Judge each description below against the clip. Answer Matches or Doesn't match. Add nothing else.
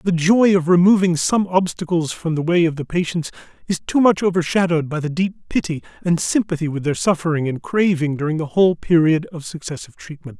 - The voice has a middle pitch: Matches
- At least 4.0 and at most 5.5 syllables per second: Doesn't match